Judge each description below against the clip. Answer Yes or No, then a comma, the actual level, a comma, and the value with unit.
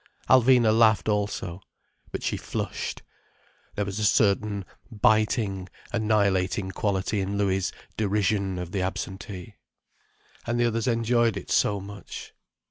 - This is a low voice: Yes, low, 105 Hz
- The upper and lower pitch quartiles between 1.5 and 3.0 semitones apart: Yes, narrow, 2.4 semitones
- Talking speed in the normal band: No, slow, 125 wpm